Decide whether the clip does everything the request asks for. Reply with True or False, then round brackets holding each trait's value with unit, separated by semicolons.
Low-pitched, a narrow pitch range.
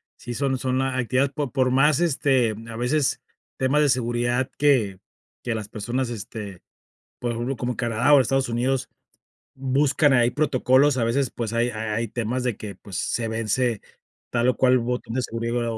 True (125 Hz; 2.3 semitones)